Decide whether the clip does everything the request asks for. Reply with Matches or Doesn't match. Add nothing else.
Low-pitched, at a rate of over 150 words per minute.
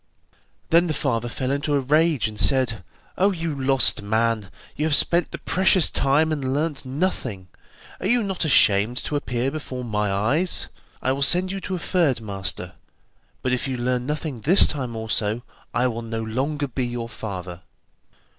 Matches